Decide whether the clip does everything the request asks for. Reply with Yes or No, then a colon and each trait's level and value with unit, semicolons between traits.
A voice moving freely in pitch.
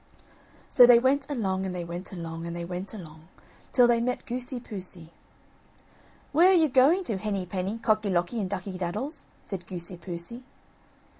Yes: wide, 5.8 semitones